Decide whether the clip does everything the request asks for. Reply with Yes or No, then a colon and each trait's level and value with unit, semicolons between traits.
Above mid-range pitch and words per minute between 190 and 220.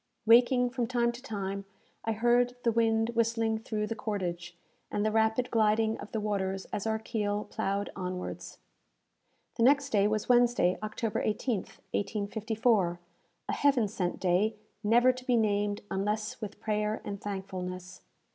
No: high, 215 Hz; average, 150 wpm